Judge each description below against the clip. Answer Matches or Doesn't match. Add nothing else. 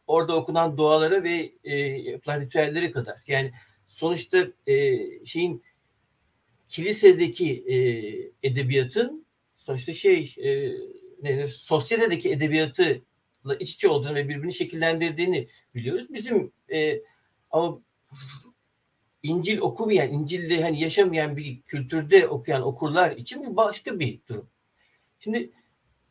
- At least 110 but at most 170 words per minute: Doesn't match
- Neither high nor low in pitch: Matches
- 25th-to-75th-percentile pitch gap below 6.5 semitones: Doesn't match